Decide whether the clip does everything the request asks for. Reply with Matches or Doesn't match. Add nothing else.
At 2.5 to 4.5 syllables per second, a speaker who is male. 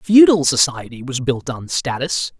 Matches